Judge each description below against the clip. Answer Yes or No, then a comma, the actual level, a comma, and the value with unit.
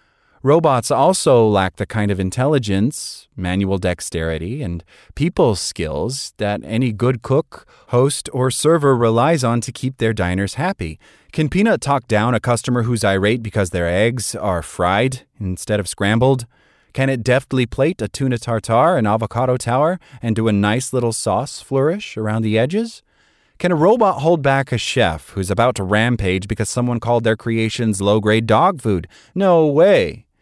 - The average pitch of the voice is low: Yes, low, 115 Hz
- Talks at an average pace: Yes, average, 165 wpm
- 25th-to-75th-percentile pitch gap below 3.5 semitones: No, average, 4.3 semitones